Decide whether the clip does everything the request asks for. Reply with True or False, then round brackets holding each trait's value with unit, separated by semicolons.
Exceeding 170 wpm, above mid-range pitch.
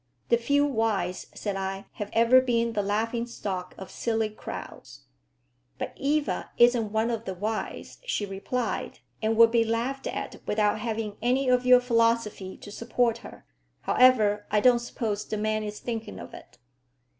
False (165 wpm; 225 Hz)